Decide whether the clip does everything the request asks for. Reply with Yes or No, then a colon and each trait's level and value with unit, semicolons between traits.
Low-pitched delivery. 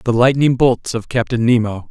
Yes: low, 120 Hz